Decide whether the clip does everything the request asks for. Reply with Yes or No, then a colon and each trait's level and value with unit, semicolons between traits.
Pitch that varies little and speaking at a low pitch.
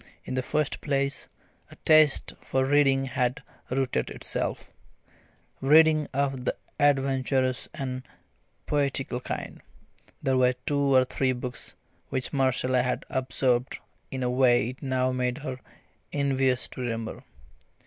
Yes: narrow, 1.5 semitones; low, 130 Hz